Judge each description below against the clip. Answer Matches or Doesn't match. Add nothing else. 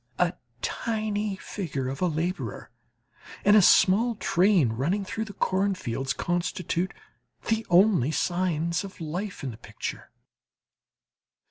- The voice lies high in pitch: Doesn't match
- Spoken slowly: Matches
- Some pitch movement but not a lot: Matches